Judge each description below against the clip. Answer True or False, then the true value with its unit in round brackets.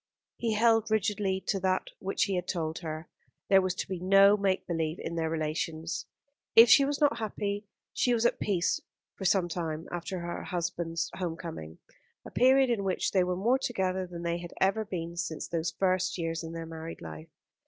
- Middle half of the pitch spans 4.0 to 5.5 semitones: False (3.4 semitones)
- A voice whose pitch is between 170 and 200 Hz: True (185 Hz)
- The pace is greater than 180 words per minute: True (195 wpm)